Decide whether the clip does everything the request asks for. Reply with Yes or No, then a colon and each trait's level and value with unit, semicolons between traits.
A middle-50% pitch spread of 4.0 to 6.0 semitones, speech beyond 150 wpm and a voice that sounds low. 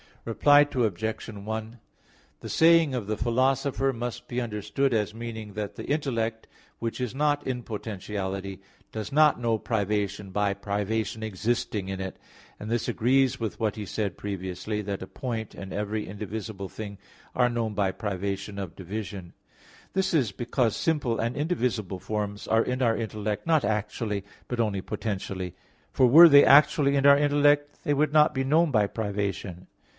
Yes: average, 4.3 semitones; average, 160 wpm; low, 110 Hz